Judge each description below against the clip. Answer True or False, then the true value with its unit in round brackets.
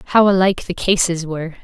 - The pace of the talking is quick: False (185 wpm)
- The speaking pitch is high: False (180 Hz)